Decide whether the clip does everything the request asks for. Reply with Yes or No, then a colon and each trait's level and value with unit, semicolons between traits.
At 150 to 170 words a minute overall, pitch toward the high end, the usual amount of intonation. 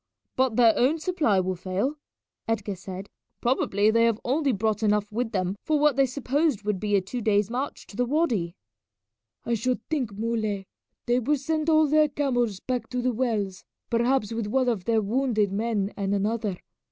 No: average, 185 wpm; high, 230 Hz; average, 4.2 semitones